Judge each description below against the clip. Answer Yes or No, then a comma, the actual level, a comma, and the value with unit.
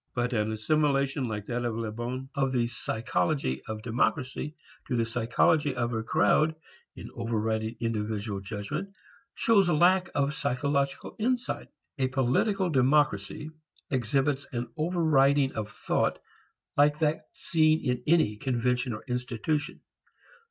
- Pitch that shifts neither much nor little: Yes, average, 4.6 semitones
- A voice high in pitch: No, low, 130 Hz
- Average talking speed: No, slow, 130 wpm